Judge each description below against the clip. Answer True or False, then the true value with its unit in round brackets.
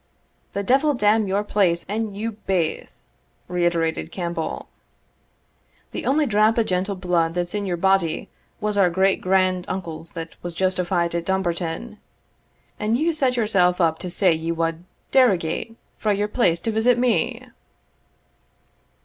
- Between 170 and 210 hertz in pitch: True (190 Hz)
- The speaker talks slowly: False (150 wpm)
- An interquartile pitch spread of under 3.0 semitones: False (3.9 semitones)